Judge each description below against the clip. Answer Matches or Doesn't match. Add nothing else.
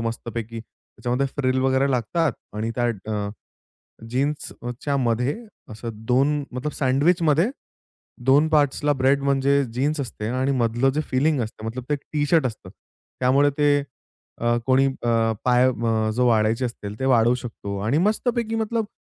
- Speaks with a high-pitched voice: Doesn't match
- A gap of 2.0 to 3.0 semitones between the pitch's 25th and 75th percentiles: Doesn't match